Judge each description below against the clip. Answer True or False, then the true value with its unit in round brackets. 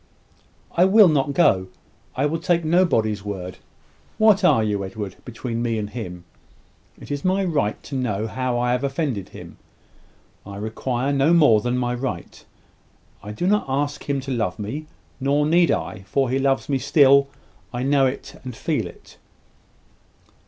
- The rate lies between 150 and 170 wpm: True (165 wpm)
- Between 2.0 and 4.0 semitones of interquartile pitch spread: False (5.0 semitones)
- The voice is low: True (130 Hz)